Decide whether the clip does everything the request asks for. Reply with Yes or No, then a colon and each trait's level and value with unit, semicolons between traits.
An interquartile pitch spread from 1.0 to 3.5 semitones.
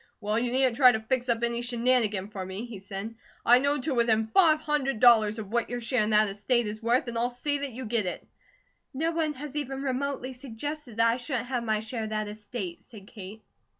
Yes: average, 3.2 semitones